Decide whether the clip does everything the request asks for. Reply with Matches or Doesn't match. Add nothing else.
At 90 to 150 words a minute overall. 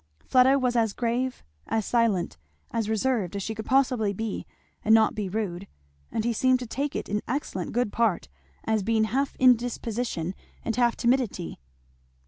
Doesn't match